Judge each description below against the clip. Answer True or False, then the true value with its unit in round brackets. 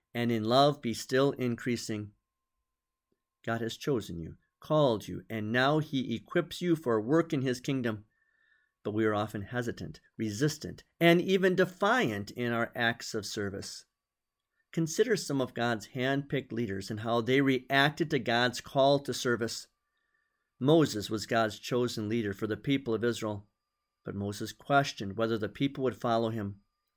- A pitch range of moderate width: True (4.5 semitones)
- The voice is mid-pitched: False (120 Hz)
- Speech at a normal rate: True (160 wpm)